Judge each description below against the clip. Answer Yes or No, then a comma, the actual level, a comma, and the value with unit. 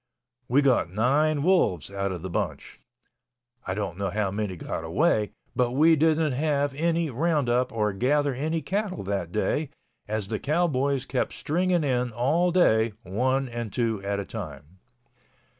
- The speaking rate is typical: Yes, average, 150 wpm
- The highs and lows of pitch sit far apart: Yes, wide, 6.9 semitones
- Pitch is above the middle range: No, low, 125 Hz